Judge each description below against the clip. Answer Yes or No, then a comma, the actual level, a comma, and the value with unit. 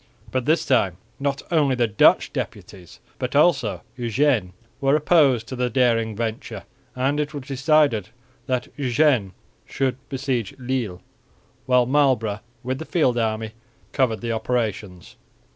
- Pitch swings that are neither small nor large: Yes, average, 3.7 semitones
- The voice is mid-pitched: No, low, 125 Hz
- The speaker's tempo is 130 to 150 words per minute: Yes, slow, 135 wpm